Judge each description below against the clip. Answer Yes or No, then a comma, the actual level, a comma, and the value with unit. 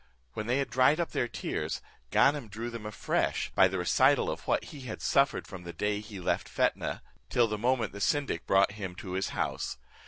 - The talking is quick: Yes, fast, 210 wpm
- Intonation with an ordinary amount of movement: Yes, average, 4.7 semitones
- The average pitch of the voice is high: No, low, 105 Hz